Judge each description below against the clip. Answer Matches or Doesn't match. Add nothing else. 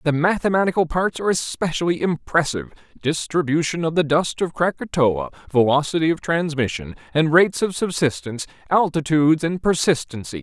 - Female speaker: Doesn't match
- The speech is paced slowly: Matches